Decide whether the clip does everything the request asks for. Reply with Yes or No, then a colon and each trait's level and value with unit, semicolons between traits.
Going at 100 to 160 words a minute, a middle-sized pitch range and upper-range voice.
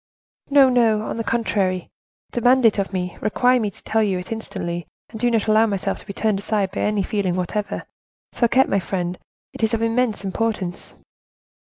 No: average, 195 wpm; average, 3.0 semitones; high, 215 Hz